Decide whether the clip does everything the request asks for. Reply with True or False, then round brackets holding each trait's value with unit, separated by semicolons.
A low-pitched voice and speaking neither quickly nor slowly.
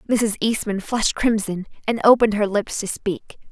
False (210 Hz; 170 wpm)